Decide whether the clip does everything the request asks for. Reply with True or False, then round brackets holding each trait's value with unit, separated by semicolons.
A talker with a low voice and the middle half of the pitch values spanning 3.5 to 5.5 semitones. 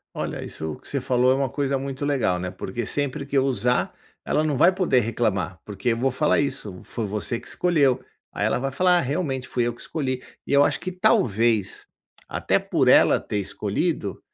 True (130 Hz; 4.1 semitones)